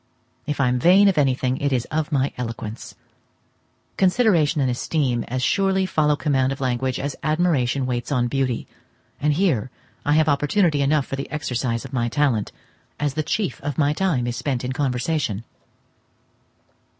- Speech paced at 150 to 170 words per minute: Yes, average, 165 wpm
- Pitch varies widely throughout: No, average, 3.5 semitones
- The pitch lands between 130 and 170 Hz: Yes, medium, 140 Hz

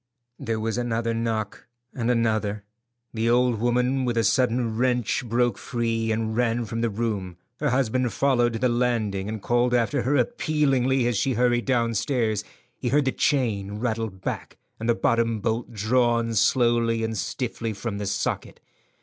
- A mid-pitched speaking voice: No, low, 115 Hz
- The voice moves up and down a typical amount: No, narrow, 1.9 semitones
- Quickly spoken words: No, average, 165 wpm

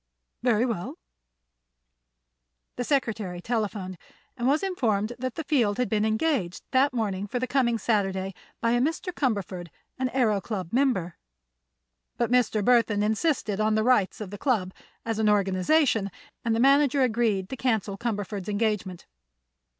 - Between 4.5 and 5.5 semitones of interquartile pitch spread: No, average, 4.0 semitones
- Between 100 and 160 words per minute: Yes, average, 150 wpm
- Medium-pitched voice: No, high, 220 Hz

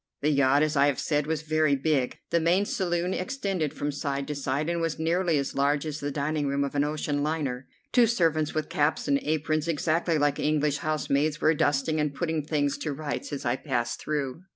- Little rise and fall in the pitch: Yes, narrow, 2.1 semitones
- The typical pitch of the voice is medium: Yes, medium, 150 Hz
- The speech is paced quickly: Yes, fast, 210 wpm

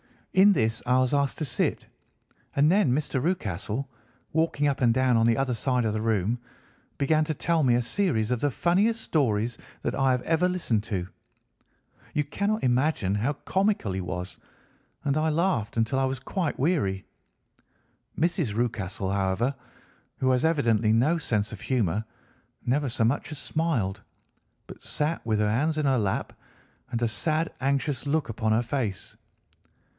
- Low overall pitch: Yes, low, 130 Hz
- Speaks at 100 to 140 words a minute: No, average, 170 wpm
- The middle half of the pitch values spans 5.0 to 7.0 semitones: Yes, wide, 5.6 semitones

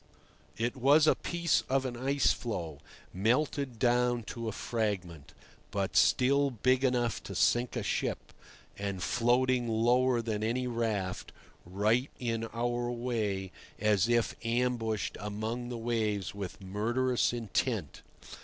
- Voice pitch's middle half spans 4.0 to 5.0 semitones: No, average, 2.8 semitones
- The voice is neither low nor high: No, low, 120 Hz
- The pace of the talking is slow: Yes, slow, 130 wpm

